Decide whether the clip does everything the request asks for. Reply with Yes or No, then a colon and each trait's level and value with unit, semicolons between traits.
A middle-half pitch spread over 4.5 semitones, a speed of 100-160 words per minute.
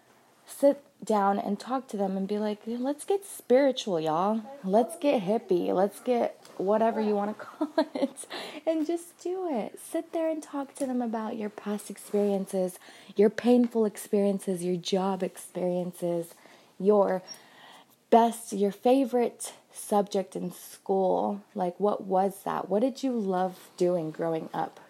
Yes: average, 5.2 semitones; average, 150 wpm